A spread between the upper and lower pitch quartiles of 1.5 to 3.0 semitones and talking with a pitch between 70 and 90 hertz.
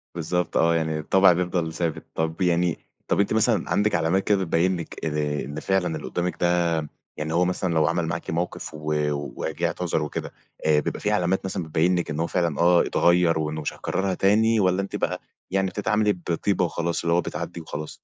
Yes: narrow, 2.4 semitones; very low, 85 Hz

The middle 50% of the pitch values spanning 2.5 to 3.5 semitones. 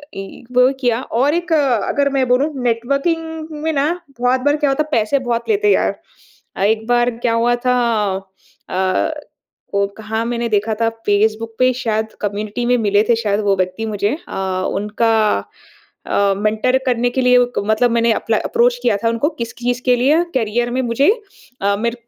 Yes: average, 2.9 semitones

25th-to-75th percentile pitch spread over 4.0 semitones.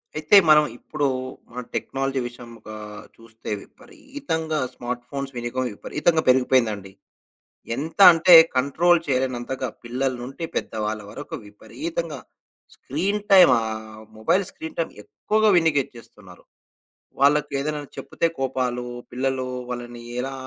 Yes: average, 4.7 semitones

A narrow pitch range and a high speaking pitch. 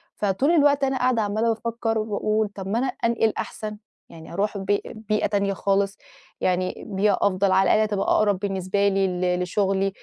Yes: narrow, 2.2 semitones; high, 205 Hz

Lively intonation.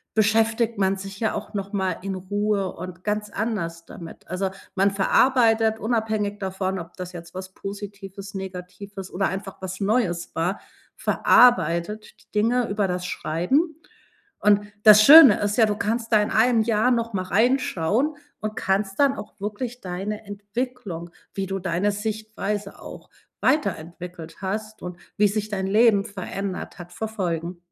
No: average, 2.7 semitones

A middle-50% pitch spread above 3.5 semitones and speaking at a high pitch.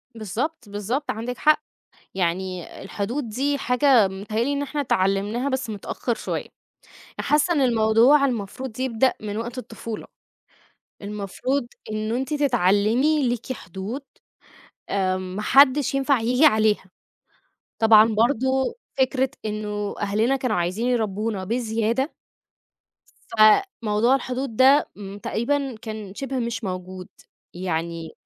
Yes: average, 4.2 semitones; high, 230 Hz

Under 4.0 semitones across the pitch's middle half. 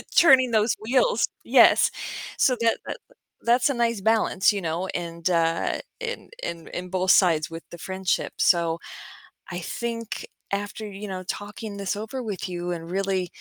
No: average, 4.3 semitones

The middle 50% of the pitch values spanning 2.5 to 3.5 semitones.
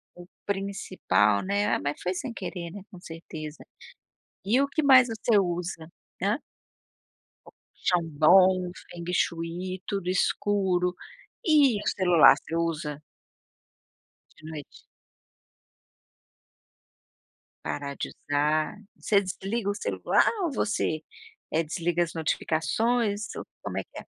No: average, 3.9 semitones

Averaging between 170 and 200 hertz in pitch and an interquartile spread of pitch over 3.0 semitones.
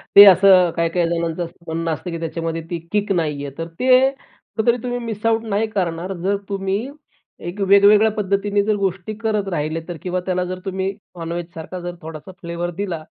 Yes: medium, 185 Hz; average, 3.4 semitones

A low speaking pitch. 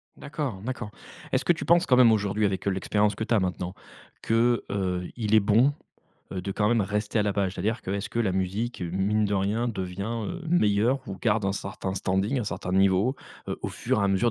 Yes: low, 105 Hz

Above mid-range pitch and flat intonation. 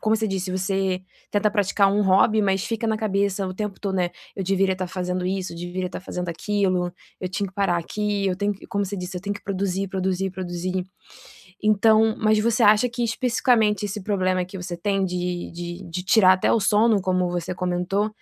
Yes: high, 195 Hz; narrow, 2.3 semitones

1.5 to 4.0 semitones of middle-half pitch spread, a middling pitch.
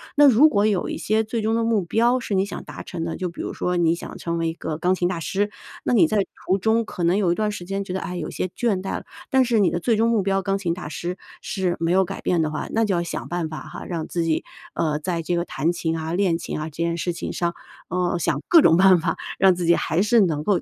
Yes: average, 3.5 semitones; medium, 180 Hz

